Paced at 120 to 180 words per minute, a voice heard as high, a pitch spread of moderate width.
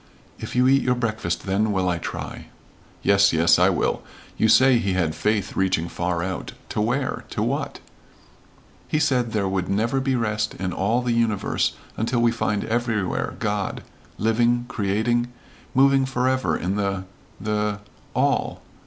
No: average, 155 wpm; low, 110 Hz; average, 3.8 semitones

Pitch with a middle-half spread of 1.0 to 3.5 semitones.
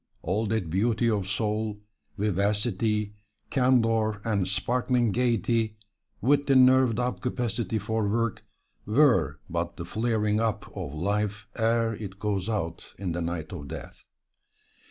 Yes: average, 3.1 semitones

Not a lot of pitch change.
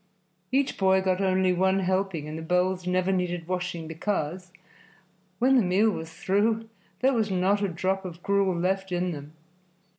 Yes: narrow, 1.7 semitones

